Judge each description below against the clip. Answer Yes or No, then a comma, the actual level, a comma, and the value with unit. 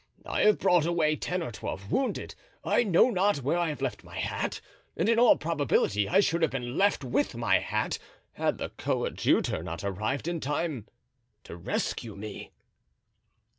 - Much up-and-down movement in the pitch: Yes, wide, 7.0 semitones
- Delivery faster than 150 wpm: Yes, average, 170 wpm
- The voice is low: No, medium, 150 Hz